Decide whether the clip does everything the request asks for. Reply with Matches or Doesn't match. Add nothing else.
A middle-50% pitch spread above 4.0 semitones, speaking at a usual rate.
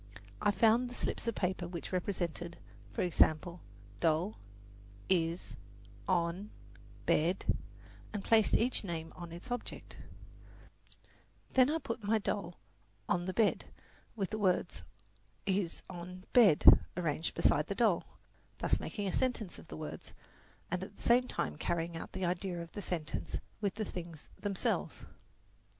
Doesn't match